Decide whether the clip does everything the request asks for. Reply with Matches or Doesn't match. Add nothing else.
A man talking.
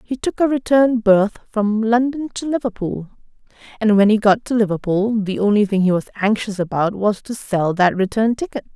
Doesn't match